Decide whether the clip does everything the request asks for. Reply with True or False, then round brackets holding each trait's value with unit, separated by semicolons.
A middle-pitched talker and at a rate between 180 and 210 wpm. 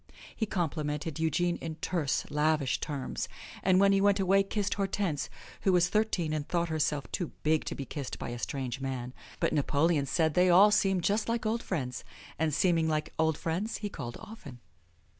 True (165 Hz; 185 wpm)